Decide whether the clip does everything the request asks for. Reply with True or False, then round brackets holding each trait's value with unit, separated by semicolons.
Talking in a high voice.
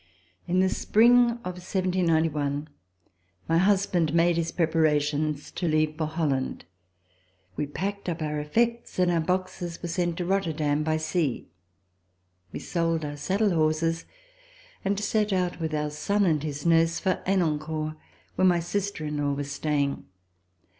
False (165 Hz)